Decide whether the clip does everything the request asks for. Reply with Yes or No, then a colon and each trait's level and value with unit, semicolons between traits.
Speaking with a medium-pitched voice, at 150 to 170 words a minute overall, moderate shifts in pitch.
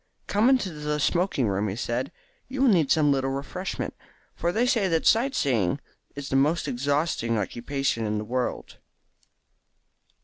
No: medium, 145 Hz; average, 160 wpm; wide, 6.8 semitones